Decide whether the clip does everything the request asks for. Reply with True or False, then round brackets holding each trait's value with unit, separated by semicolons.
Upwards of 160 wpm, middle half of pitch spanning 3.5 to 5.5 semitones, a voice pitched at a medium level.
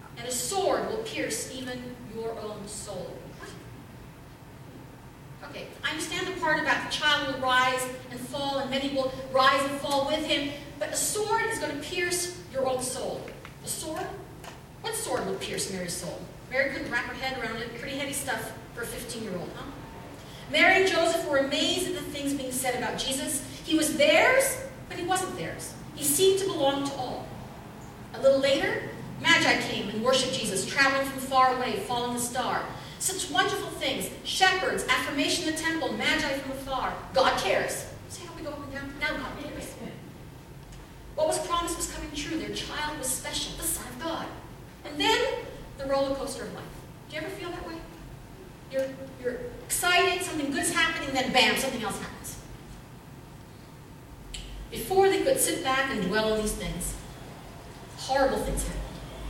False (180 wpm; 4.7 semitones; 275 Hz)